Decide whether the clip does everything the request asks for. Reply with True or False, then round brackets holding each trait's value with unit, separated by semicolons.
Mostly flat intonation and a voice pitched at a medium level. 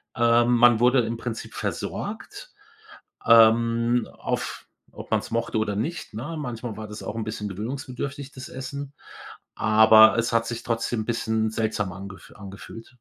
False (2.0 semitones; 115 Hz)